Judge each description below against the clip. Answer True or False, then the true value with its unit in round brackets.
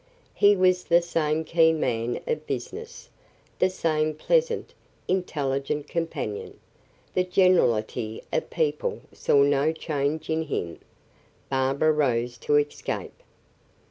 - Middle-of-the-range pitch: True (155 Hz)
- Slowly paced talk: True (110 wpm)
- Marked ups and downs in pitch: False (4.8 semitones)